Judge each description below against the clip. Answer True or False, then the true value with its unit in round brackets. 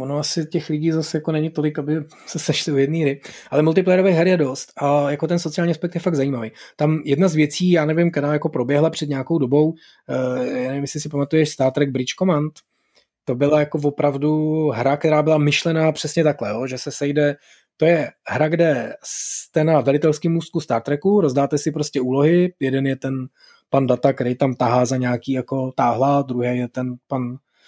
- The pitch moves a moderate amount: True (3.0 semitones)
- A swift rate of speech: True (200 wpm)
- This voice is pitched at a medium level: True (150 Hz)